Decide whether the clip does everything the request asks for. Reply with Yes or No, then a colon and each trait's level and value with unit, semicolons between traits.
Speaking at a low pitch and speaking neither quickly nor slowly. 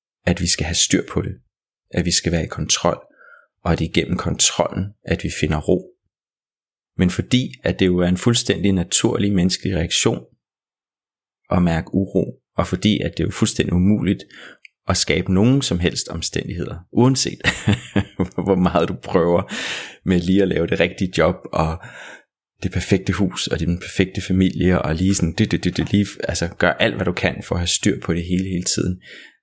Yes: very low, 90 Hz; average, 195 wpm